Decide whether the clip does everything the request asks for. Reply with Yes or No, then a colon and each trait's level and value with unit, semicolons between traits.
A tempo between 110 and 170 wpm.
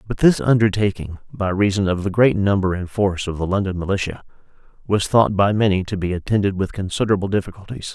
No: average, 190 wpm